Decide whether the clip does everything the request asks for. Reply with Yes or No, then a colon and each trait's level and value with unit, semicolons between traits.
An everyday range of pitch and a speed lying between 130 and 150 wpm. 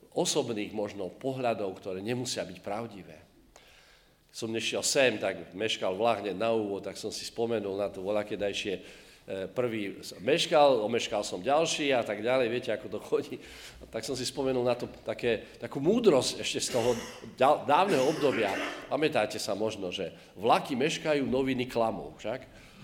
Yes: average, 3.5 semitones; average, 145 wpm